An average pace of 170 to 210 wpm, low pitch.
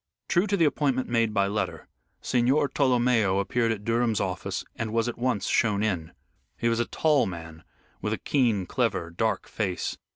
Yes: average, 175 wpm; low, 115 Hz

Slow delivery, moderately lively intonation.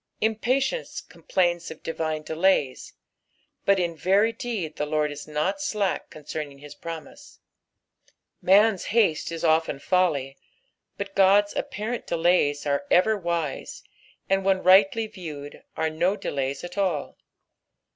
Yes: slow, 125 wpm; average, 4.6 semitones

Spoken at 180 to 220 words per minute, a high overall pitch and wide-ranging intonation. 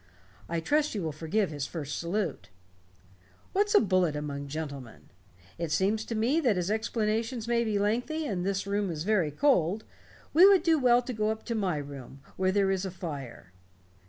Yes: average, 190 wpm; high, 195 Hz; wide, 6.3 semitones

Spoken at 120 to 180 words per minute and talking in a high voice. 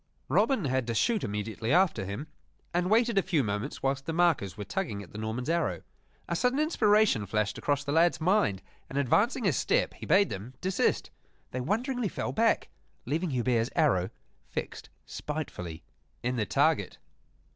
No: average, 165 wpm; medium, 145 Hz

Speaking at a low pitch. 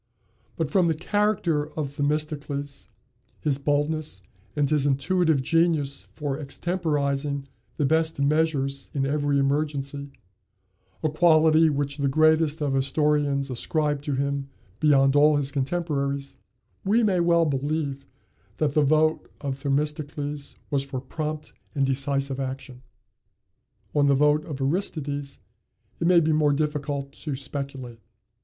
No: medium, 145 Hz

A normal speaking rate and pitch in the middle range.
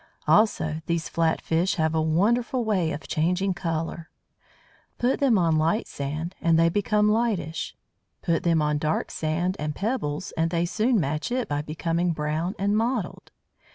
Yes: average, 160 wpm; medium, 170 Hz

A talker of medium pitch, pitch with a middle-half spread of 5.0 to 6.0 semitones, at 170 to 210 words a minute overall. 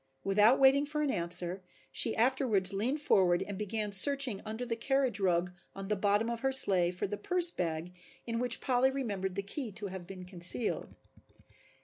No: high, 210 Hz; wide, 5.4 semitones; average, 185 wpm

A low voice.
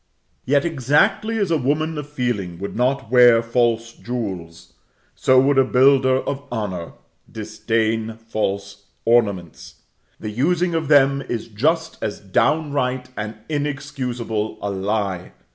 Yes: low, 125 Hz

